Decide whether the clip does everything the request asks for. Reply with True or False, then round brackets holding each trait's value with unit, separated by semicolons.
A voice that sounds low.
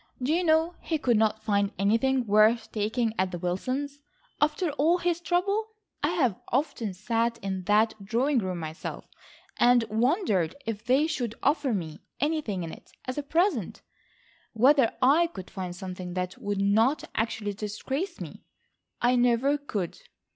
False (235 Hz)